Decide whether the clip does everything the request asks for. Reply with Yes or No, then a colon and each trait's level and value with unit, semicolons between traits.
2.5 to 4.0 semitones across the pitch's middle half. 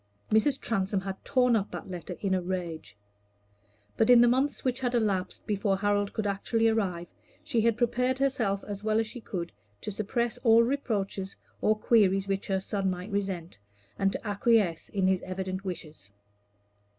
Yes: average, 3.3 semitones